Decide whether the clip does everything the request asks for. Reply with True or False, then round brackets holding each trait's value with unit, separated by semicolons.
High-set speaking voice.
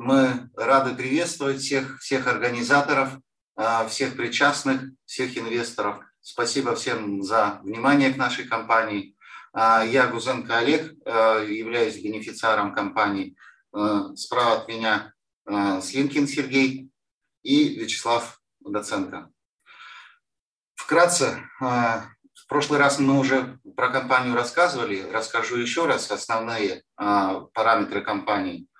False (130 Hz)